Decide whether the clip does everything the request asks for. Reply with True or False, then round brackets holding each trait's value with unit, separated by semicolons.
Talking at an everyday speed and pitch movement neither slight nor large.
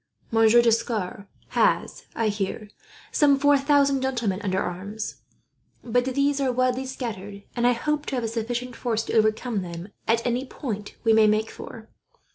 True (165 wpm; 3.3 semitones)